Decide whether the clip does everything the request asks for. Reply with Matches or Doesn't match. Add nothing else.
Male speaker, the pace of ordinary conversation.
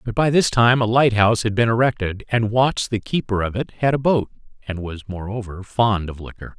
Doesn't match